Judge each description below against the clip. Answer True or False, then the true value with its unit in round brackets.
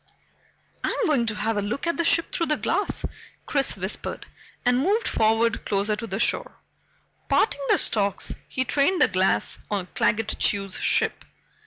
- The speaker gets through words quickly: False (165 wpm)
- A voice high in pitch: True (225 Hz)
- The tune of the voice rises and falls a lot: True (6.1 semitones)